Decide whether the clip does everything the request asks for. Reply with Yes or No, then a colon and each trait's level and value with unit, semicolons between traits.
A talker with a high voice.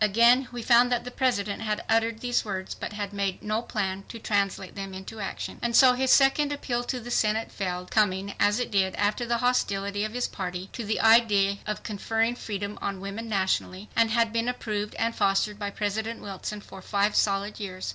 Yes: high, 210 Hz